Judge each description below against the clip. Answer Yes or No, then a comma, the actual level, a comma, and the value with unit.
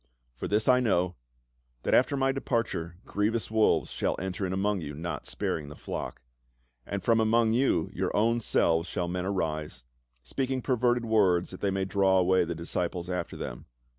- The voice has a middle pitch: No, very low, 95 Hz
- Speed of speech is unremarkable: Yes, average, 180 wpm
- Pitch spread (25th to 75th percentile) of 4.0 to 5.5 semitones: Yes, average, 4.7 semitones